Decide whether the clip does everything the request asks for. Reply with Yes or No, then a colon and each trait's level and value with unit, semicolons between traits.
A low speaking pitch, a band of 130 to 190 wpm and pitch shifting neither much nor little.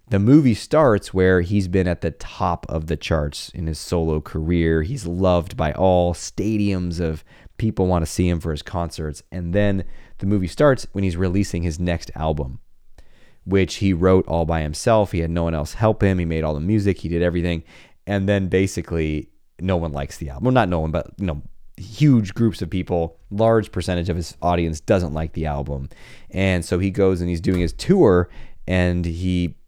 No: very low, 90 Hz; fast, 205 wpm; average, 3.0 semitones